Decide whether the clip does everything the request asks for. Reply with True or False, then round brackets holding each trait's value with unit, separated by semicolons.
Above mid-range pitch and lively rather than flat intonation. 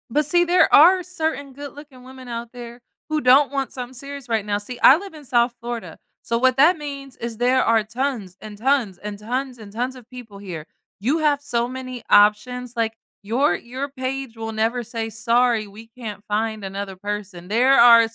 False (245 Hz; 3.7 semitones)